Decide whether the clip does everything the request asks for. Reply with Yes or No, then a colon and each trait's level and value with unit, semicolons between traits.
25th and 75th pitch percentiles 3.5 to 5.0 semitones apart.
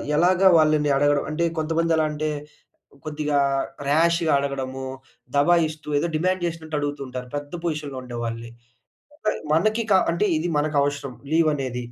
No: average, 2.8 semitones